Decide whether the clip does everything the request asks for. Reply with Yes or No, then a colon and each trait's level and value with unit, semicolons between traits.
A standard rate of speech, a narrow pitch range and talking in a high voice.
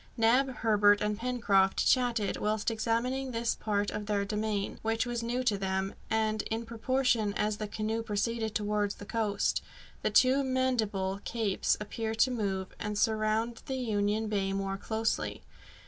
Yes: average, 150 wpm; narrow, 2.1 semitones; high, 220 Hz